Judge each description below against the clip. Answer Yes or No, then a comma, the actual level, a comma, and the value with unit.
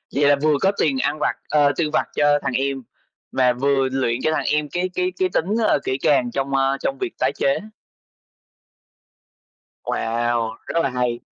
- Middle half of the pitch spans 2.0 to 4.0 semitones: Yes, average, 2.9 semitones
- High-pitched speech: No, medium, 140 Hz